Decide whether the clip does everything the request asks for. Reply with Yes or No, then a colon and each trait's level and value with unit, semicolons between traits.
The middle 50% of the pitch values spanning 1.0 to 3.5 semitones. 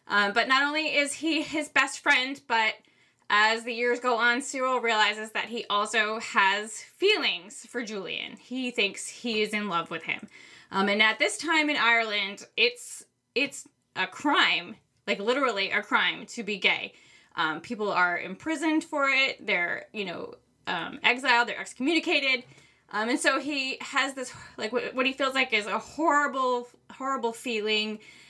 No: average, 4.6 semitones